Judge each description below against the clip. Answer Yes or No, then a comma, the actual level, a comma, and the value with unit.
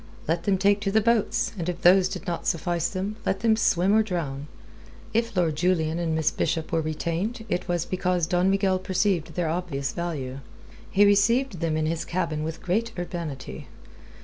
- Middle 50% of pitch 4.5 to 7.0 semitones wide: No, average, 3.4 semitones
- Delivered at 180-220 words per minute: Yes, average, 185 wpm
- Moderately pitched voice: Yes, medium, 175 Hz